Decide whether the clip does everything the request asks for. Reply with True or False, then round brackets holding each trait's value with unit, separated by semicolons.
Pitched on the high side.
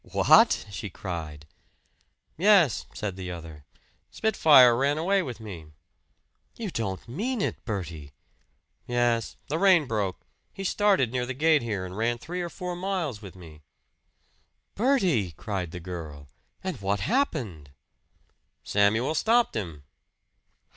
False (115 Hz)